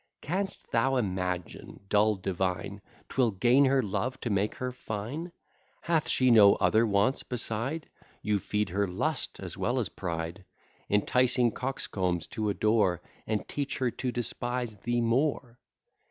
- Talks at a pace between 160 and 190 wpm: No, average, 140 wpm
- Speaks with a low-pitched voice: Yes, low, 110 Hz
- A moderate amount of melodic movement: Yes, average, 4.2 semitones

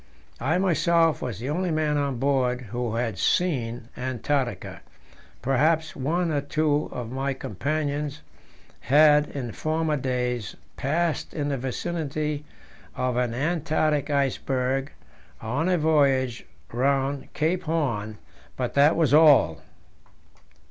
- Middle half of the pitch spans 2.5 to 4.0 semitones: Yes, average, 3.6 semitones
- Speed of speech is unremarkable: No, slow, 120 wpm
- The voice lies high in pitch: No, medium, 140 Hz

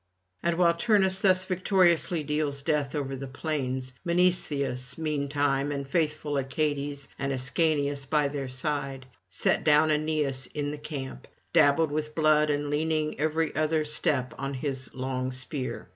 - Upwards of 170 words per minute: No, average, 145 wpm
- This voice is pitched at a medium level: Yes, medium, 145 Hz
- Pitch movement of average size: No, narrow, 2.3 semitones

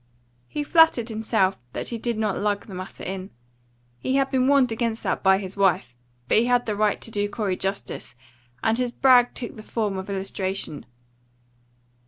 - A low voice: No, high, 215 Hz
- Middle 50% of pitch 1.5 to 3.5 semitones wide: No, average, 3.9 semitones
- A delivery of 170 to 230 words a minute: Yes, average, 185 wpm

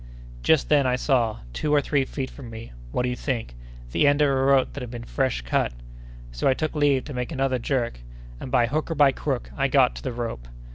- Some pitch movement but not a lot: Yes, average, 3.1 semitones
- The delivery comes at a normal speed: No, fast, 230 wpm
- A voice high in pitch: No, low, 130 Hz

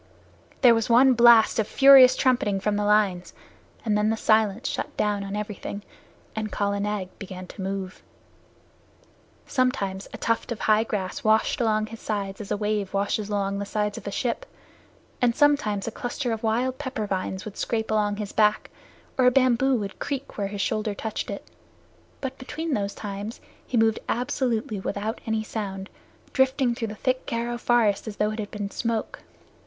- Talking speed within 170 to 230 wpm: Yes, average, 180 wpm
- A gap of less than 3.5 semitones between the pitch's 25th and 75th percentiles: Yes, average, 2.8 semitones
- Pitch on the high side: Yes, high, 215 Hz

